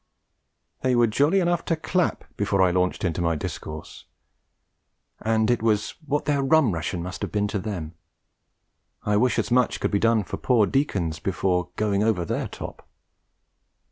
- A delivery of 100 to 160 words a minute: No, average, 170 wpm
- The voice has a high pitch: No, low, 105 Hz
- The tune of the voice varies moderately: No, wide, 5.7 semitones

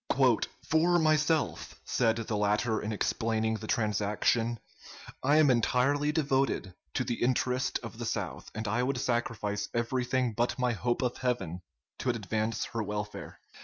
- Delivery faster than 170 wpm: No, average, 145 wpm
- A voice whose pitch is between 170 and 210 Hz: No, low, 120 Hz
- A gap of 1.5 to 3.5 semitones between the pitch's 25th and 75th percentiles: Yes, average, 3.1 semitones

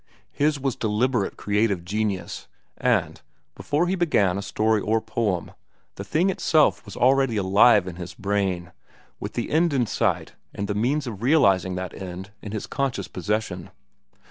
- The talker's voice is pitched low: Yes, low, 105 Hz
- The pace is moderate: Yes, average, 160 wpm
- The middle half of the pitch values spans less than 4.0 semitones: No, average, 5.3 semitones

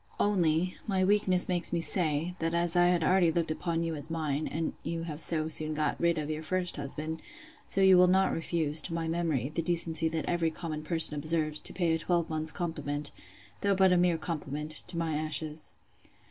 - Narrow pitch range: Yes, narrow, 2.0 semitones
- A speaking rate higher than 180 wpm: Yes, average, 200 wpm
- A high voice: No, medium, 165 Hz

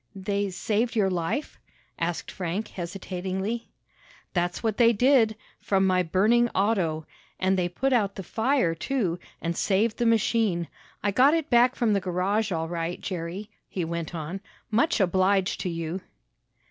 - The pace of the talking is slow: No, average, 155 wpm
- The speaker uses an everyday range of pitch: Yes, average, 4.2 semitones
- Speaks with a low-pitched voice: No, high, 195 Hz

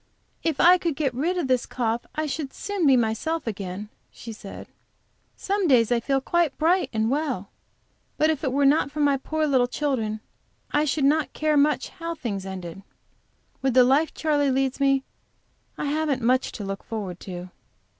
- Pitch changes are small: No, average, 5.1 semitones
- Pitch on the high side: Yes, very high, 275 Hz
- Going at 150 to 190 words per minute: Yes, average, 185 wpm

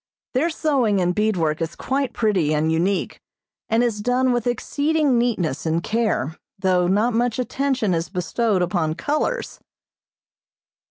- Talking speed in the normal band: Yes, average, 145 wpm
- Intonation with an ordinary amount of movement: No, wide, 5.8 semitones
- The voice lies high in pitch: Yes, high, 215 Hz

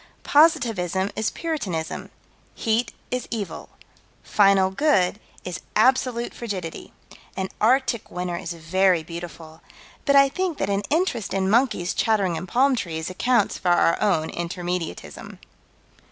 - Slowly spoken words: Yes, slow, 125 wpm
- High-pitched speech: Yes, high, 195 Hz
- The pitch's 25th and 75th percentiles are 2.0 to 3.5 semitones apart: No, wide, 5.6 semitones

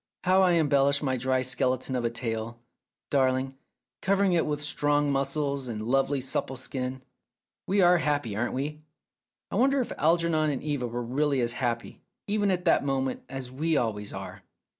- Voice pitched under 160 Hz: Yes, low, 135 Hz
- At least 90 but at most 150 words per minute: No, average, 175 wpm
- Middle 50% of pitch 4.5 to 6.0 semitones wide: No, average, 3.4 semitones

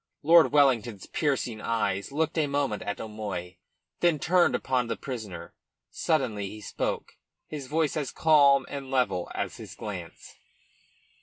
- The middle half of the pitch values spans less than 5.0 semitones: No, wide, 5.6 semitones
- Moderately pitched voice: No, low, 130 Hz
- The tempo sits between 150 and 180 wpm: No, average, 140 wpm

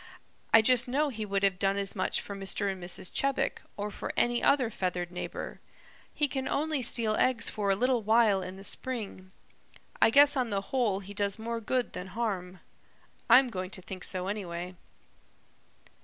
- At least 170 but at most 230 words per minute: Yes, average, 185 wpm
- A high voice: Yes, high, 210 Hz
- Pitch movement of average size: Yes, average, 4.2 semitones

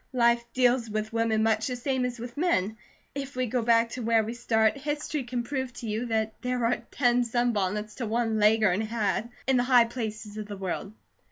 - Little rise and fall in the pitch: Yes, narrow, 2.3 semitones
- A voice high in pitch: Yes, high, 235 Hz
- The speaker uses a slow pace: No, fast, 205 wpm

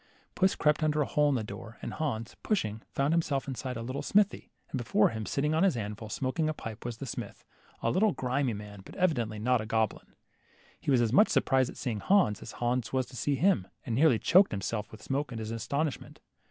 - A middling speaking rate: No, fast, 220 wpm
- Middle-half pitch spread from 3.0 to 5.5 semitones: Yes, average, 5.1 semitones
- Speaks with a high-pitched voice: No, low, 125 Hz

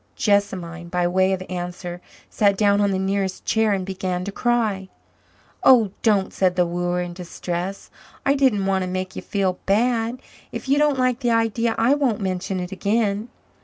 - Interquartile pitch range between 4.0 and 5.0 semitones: No, average, 3.6 semitones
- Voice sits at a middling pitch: No, high, 195 Hz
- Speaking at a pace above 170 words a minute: Yes, average, 180 wpm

